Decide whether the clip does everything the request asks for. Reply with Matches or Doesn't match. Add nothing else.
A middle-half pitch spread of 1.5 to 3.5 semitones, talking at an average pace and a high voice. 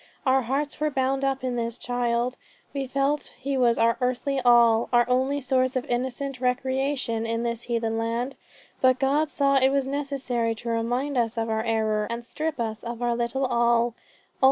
Matches